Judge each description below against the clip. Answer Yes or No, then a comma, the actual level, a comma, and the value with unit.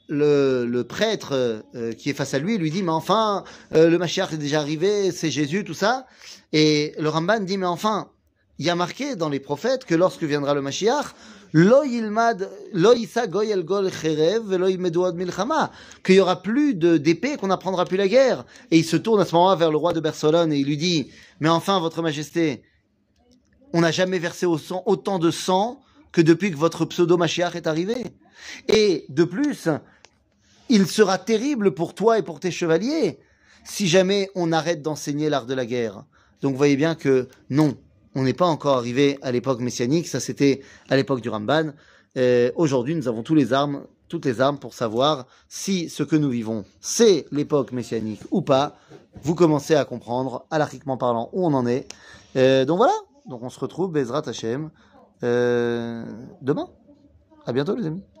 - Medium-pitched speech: Yes, medium, 160 Hz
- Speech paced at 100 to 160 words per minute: No, average, 180 wpm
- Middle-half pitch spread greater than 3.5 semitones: Yes, wide, 5.6 semitones